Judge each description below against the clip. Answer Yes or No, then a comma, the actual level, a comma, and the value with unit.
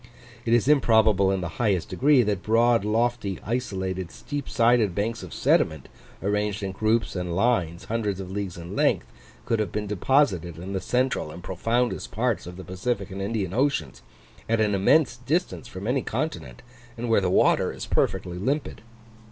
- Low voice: Yes, low, 105 Hz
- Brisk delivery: No, average, 175 wpm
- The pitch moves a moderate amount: Yes, average, 4.3 semitones